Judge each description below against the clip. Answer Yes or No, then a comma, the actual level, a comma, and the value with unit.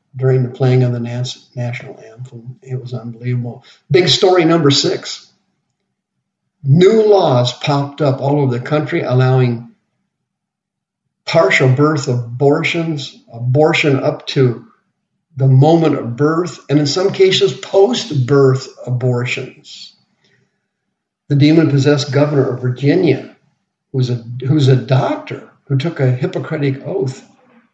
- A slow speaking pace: Yes, slow, 115 wpm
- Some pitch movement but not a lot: Yes, average, 4.0 semitones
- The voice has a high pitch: No, medium, 140 Hz